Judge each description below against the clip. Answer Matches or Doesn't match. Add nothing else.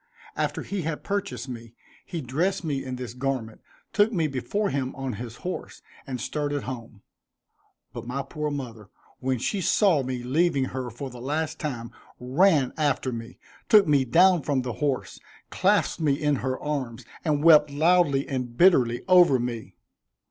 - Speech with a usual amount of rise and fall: Matches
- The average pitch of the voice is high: Doesn't match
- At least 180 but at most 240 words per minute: Doesn't match